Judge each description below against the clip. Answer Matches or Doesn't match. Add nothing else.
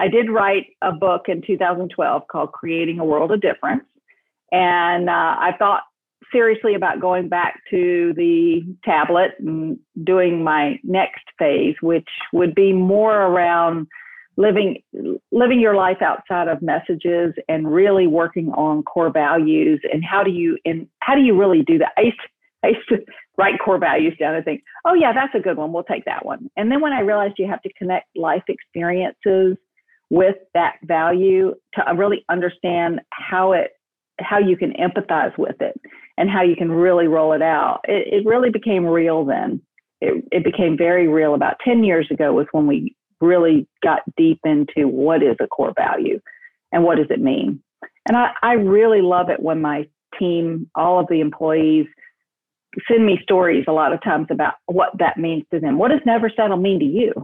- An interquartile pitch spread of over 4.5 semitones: Matches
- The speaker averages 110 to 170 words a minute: Doesn't match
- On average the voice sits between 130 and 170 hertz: Doesn't match